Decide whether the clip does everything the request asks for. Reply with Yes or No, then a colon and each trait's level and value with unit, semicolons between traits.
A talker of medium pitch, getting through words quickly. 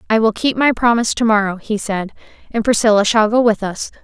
No: high, 220 Hz; fast, 225 wpm